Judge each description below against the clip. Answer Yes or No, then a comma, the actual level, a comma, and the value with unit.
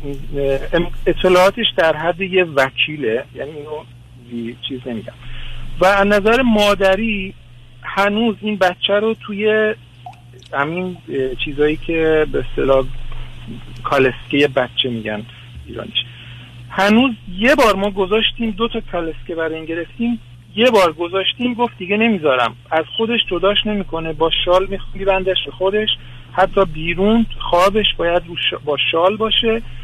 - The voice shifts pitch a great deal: Yes, wide, 8.2 semitones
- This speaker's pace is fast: No, average, 120 wpm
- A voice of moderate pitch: Yes, medium, 170 Hz